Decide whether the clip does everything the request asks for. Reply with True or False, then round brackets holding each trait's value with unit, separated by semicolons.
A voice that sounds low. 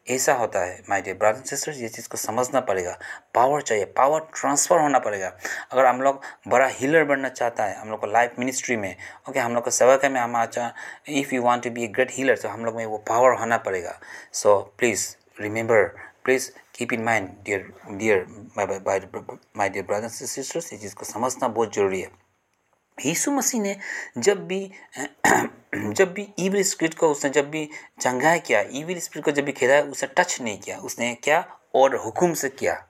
True (130 Hz)